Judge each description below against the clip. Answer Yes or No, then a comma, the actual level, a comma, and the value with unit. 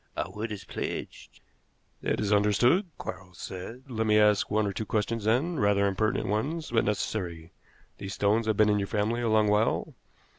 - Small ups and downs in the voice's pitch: Yes, narrow, 1.9 semitones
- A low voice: Yes, low, 105 Hz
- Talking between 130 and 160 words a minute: No, average, 185 wpm